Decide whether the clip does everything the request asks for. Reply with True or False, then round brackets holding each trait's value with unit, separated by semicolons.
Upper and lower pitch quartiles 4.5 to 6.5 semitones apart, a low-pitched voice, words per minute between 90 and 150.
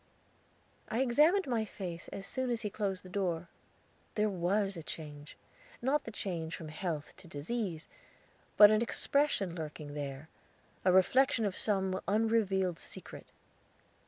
False (5.1 semitones; 195 Hz; 140 wpm)